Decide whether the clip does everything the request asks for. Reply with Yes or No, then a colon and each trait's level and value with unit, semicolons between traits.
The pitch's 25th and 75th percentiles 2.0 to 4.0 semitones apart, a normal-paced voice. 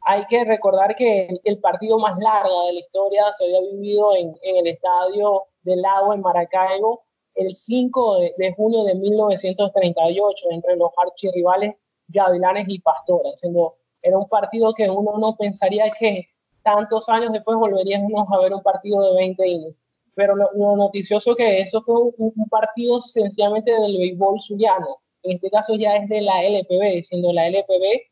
Yes: narrow, 2.6 semitones; average, 170 wpm